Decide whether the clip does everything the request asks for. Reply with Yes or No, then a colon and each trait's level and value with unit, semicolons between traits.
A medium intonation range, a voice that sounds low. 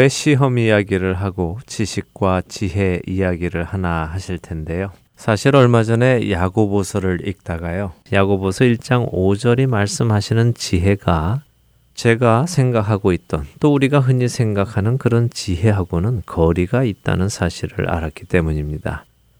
Yes: average, 4.5 semitones; low, 100 Hz